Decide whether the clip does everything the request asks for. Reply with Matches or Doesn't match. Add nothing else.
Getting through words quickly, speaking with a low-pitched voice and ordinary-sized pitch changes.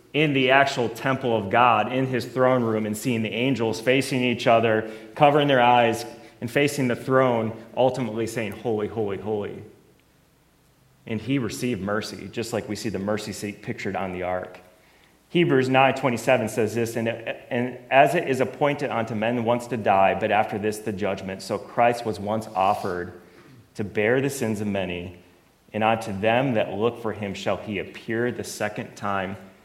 Doesn't match